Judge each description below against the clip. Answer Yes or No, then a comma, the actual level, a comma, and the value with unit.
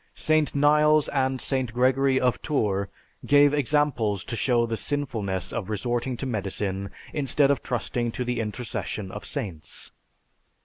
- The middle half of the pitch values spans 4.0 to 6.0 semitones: Yes, average, 4.7 semitones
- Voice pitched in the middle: No, low, 125 Hz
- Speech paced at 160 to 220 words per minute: No, average, 140 wpm